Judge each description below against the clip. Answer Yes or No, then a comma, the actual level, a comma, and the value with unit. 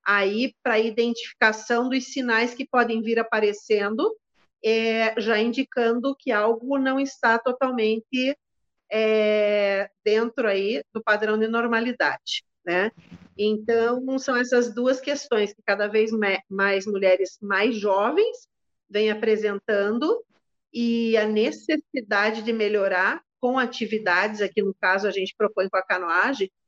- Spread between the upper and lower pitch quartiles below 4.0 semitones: Yes, average, 3.1 semitones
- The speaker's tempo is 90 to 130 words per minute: Yes, average, 125 wpm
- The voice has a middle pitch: No, high, 225 Hz